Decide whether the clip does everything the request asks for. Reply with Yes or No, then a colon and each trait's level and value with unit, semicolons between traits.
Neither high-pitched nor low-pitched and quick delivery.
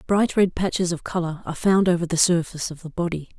Yes: medium, 175 Hz; fast, 230 wpm